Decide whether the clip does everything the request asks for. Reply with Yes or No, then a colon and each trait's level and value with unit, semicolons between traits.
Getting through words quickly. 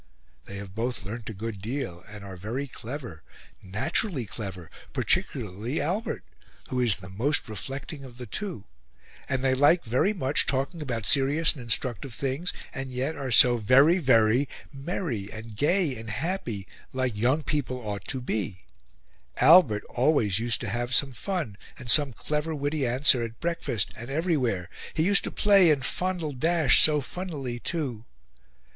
No: average, 160 wpm